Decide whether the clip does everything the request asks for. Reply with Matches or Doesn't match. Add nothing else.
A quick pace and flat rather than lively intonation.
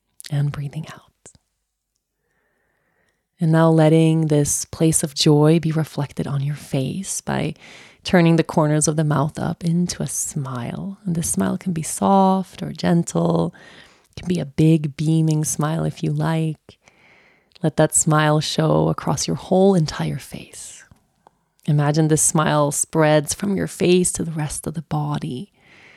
Doesn't match